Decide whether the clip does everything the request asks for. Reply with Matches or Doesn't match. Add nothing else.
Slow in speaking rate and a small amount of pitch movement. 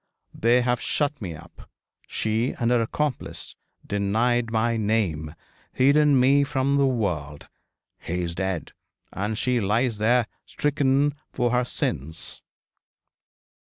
Doesn't match